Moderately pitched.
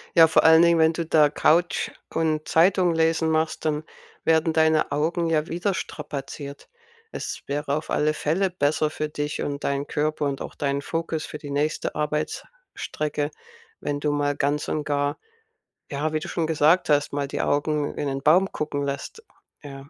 Yes: medium, 155 Hz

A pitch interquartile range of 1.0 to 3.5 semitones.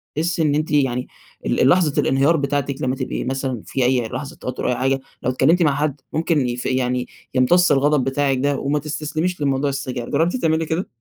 Yes: average, 2.9 semitones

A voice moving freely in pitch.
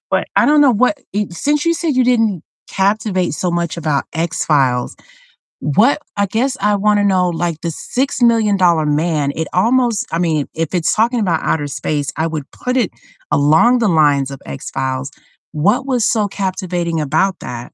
Yes: wide, 6.2 semitones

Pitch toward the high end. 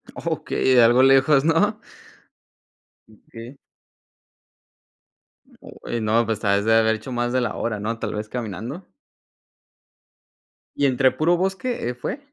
No: low, 120 Hz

